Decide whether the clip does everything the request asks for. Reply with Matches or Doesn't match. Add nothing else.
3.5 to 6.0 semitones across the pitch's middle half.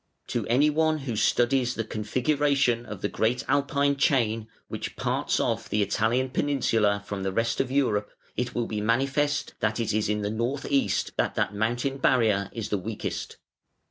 Matches